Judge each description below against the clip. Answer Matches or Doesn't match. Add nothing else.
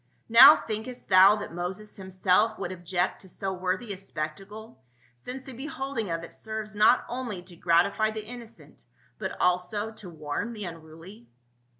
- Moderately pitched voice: Doesn't match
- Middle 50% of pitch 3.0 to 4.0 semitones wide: Matches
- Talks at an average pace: Matches